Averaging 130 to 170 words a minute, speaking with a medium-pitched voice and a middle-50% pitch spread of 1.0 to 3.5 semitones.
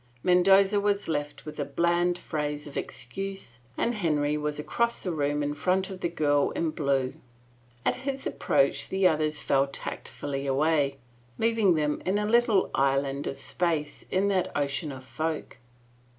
No: average, 165 wpm; medium, 155 Hz; average, 4.9 semitones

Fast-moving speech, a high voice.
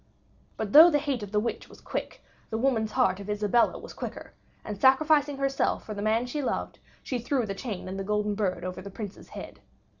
Yes: fast, 215 wpm; high, 220 Hz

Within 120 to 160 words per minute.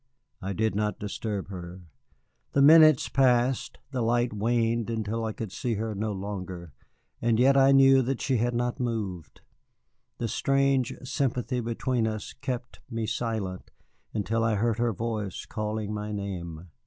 Yes: average, 155 wpm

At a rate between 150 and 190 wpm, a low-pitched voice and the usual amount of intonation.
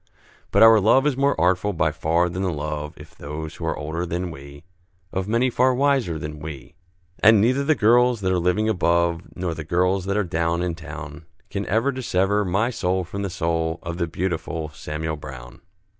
No: average, 200 wpm; very low, 90 Hz; average, 4.5 semitones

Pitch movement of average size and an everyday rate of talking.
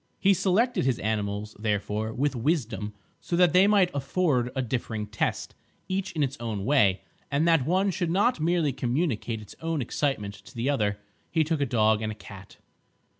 No: wide, 7.5 semitones; average, 180 wpm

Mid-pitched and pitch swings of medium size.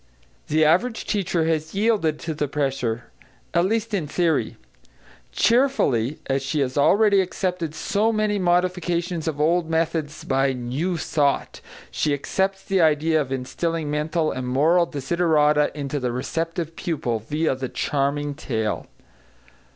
Yes: medium, 155 Hz; average, 3.9 semitones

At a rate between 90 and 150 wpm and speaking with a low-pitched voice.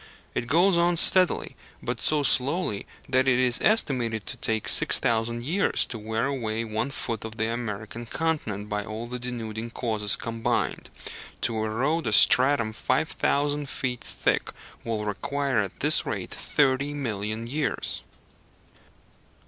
Yes: average, 140 wpm; low, 120 Hz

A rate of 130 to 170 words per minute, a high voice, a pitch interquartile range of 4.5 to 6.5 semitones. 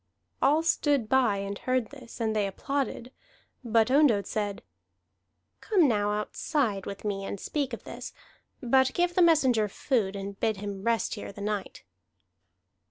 Yes: average, 155 wpm; high, 225 Hz; average, 4.9 semitones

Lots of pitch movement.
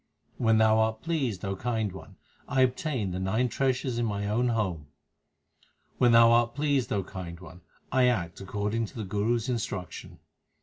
No: average, 4.1 semitones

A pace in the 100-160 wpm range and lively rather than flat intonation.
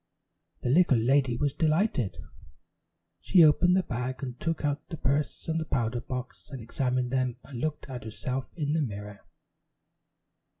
No: average, 155 wpm; average, 3.7 semitones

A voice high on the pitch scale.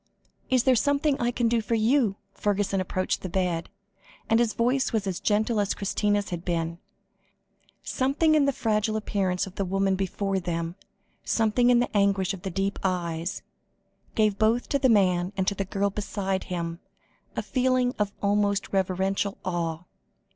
Yes: high, 200 Hz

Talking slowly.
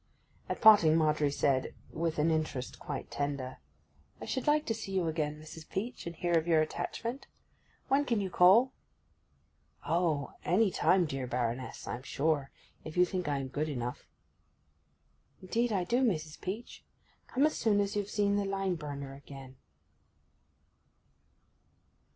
No: average, 145 wpm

